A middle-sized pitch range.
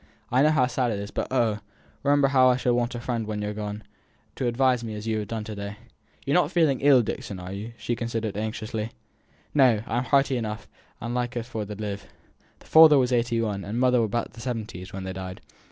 Yes: average, 3.2 semitones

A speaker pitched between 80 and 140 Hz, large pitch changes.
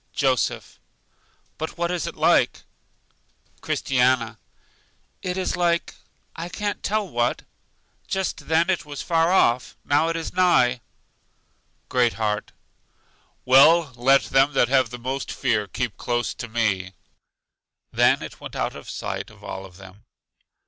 Yes: low, 135 Hz; wide, 6.0 semitones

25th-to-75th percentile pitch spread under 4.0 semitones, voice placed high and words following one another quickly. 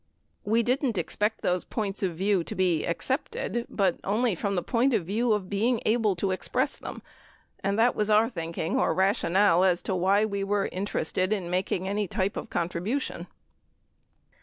No: average, 2.9 semitones; high, 200 Hz; average, 180 wpm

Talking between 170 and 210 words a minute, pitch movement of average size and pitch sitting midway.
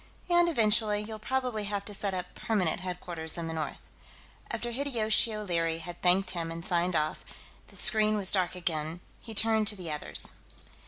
No: average, 180 wpm; average, 4.1 semitones; high, 195 Hz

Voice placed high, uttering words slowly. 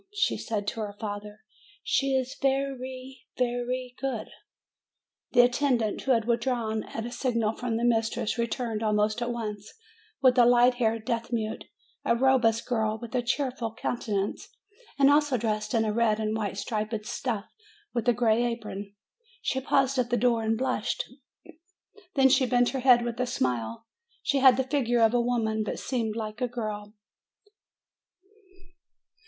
No: high, 235 Hz; average, 170 wpm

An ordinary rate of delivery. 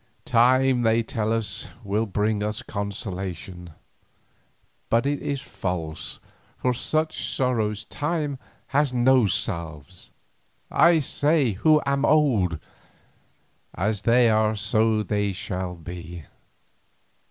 No: slow, 100 wpm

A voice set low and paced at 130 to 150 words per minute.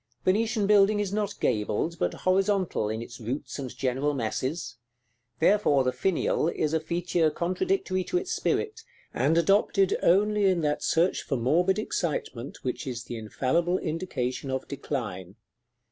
No: medium, 165 Hz; average, 145 wpm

